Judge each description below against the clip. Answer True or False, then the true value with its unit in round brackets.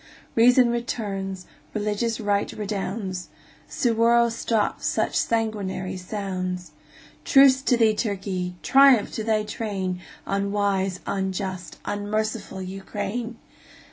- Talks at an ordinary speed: False (95 wpm)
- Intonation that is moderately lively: True (3.1 semitones)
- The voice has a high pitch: True (205 Hz)